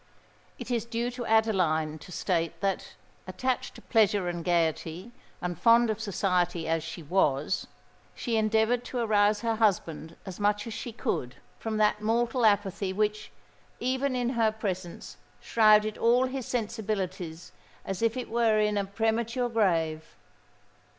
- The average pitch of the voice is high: Yes, high, 210 Hz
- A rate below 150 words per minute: Yes, average, 140 wpm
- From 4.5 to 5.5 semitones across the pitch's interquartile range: No, average, 4.1 semitones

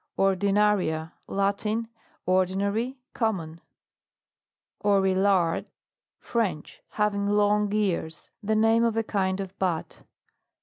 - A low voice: No, high, 200 Hz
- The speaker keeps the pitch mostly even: Yes, narrow, 2.1 semitones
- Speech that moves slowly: Yes, slow, 95 wpm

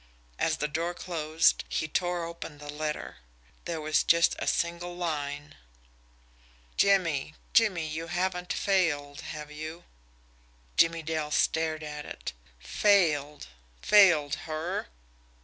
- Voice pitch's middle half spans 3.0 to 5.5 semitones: No, narrow, 2.6 semitones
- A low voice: No, medium, 160 Hz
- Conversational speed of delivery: No, slow, 115 wpm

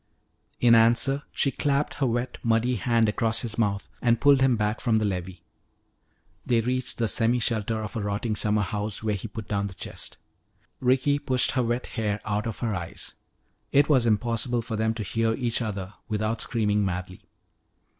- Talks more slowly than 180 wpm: No, average, 185 wpm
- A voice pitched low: Yes, low, 115 Hz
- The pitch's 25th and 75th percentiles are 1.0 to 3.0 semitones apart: Yes, narrow, 2.6 semitones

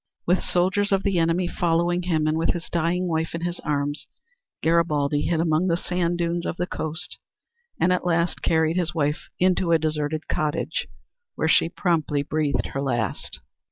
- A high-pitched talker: No, medium, 165 Hz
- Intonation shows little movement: Yes, narrow, 2.2 semitones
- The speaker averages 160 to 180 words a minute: Yes, average, 175 wpm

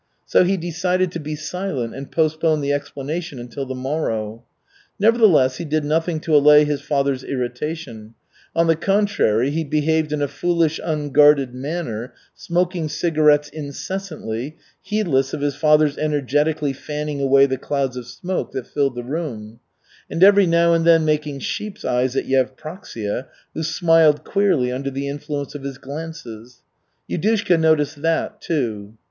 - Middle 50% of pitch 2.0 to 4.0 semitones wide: Yes, average, 3.5 semitones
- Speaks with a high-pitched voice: No, medium, 150 Hz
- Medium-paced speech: Yes, average, 150 wpm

